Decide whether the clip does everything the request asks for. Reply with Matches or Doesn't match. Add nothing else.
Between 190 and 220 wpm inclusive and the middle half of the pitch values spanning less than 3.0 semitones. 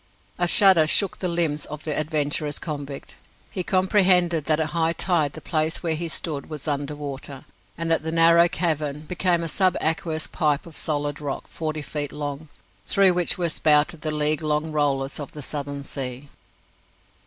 Doesn't match